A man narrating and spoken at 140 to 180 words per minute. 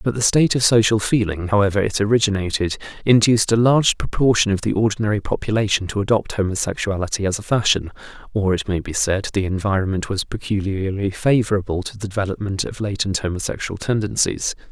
Yes: male; average, 165 wpm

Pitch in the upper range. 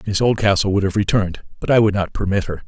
No: low, 100 Hz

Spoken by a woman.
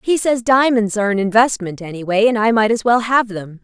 Yes: female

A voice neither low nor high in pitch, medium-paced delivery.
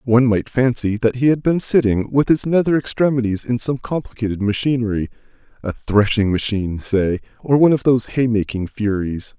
No: low, 115 Hz; average, 175 wpm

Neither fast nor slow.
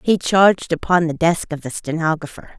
Yes: average, 185 wpm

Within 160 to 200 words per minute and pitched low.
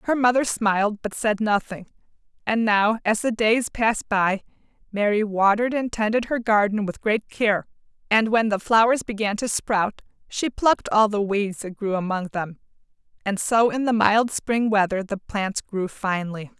No: average, 175 wpm; high, 210 Hz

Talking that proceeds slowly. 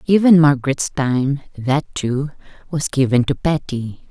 Yes: slow, 115 wpm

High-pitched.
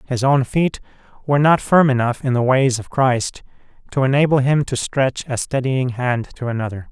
No: low, 130 Hz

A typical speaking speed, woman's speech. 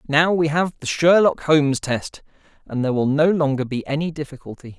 No: average, 190 wpm; male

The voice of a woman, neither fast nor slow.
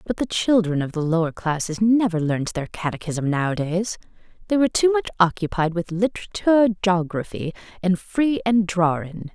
Yes: female; average, 155 wpm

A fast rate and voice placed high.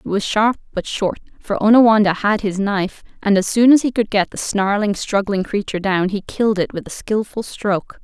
Yes: fast, 215 wpm; high, 205 Hz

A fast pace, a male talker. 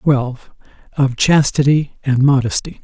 No: slow, 105 wpm; male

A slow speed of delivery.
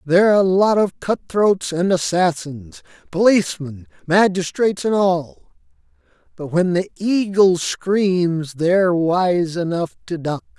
Yes: slow, 110 wpm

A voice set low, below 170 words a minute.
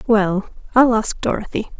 No: high, 215 Hz; slow, 135 wpm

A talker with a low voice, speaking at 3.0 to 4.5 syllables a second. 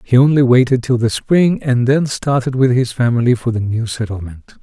No: low, 125 Hz; 5.3 syllables/s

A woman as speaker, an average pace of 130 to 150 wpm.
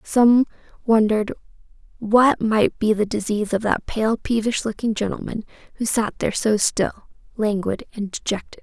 Yes: female; average, 145 wpm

